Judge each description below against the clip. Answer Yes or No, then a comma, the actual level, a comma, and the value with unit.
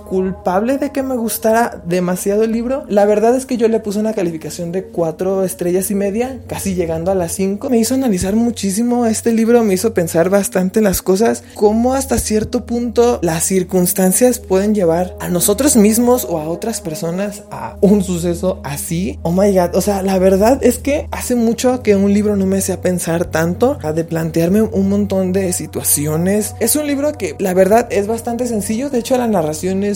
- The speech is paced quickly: Yes, fast, 200 wpm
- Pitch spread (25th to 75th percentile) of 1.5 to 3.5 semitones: No, average, 3.9 semitones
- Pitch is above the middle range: Yes, high, 200 Hz